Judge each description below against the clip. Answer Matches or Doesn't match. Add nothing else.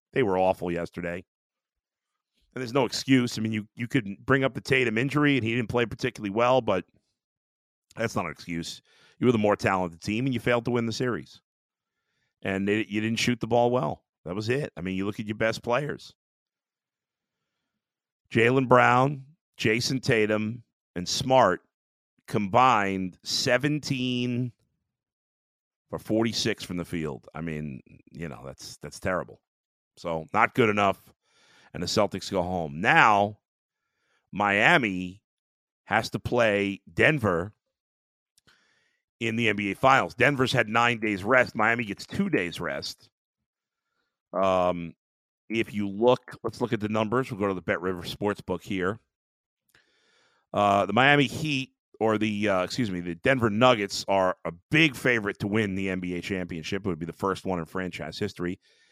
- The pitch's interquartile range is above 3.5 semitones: Matches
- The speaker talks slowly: Doesn't match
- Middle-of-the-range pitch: Doesn't match